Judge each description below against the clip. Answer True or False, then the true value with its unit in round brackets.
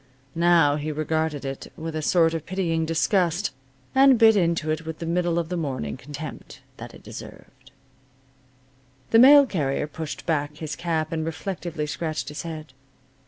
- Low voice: False (160 Hz)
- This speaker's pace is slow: False (165 wpm)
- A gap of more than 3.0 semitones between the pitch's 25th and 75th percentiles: False (2.4 semitones)